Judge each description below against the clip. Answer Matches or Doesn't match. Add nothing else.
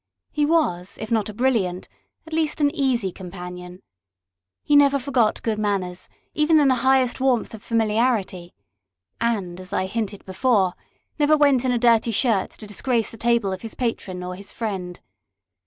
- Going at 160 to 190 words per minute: Matches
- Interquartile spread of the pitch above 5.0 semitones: Matches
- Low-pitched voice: Doesn't match